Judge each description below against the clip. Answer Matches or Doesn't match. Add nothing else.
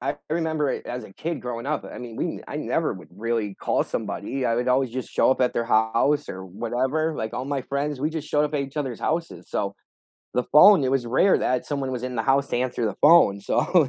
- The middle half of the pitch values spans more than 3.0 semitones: Matches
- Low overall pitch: Matches